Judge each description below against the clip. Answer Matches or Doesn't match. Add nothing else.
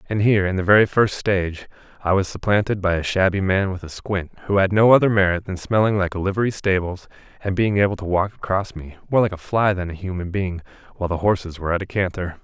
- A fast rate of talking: Matches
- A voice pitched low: Matches